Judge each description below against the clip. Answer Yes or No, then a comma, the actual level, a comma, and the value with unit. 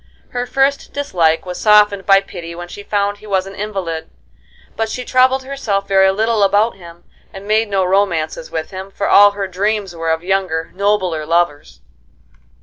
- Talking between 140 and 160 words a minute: No, average, 175 wpm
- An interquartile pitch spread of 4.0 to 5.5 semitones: No, average, 3.2 semitones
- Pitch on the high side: Yes, high, 195 Hz